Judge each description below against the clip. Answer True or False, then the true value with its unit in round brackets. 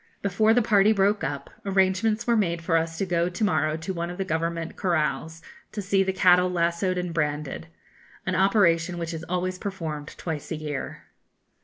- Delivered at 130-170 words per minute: False (185 wpm)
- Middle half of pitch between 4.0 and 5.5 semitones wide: False (2.9 semitones)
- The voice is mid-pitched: True (180 Hz)